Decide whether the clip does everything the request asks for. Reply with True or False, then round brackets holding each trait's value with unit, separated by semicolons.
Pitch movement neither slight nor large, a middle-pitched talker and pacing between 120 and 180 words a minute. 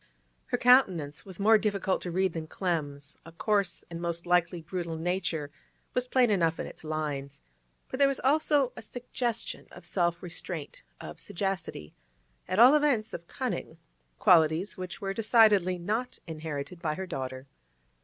True (5.0 semitones; 180 Hz; 155 wpm)